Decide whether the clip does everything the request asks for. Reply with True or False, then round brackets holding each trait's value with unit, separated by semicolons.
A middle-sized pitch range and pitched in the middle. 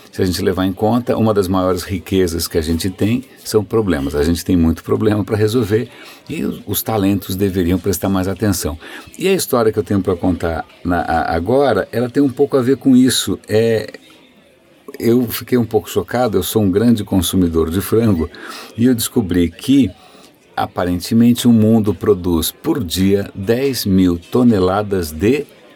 False (4.0 semitones; 100 Hz)